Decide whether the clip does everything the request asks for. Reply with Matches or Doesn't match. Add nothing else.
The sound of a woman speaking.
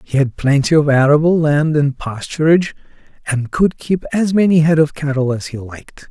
Doesn't match